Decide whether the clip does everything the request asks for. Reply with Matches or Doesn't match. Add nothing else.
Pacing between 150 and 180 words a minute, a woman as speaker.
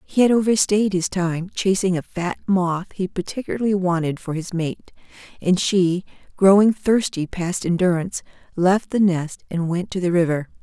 Matches